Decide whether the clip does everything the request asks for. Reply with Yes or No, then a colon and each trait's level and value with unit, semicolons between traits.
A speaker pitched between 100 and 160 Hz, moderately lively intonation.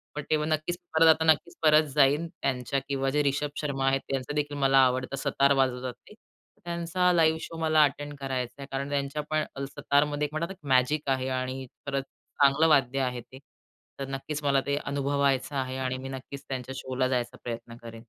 No: medium, 140 Hz; narrow, 2.1 semitones